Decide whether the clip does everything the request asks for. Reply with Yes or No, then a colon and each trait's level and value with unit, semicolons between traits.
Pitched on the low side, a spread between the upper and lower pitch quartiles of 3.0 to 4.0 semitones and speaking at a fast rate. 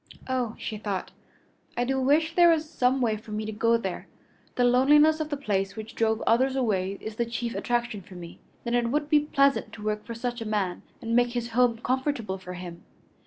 No: high, 235 Hz; average, 3.7 semitones; fast, 215 wpm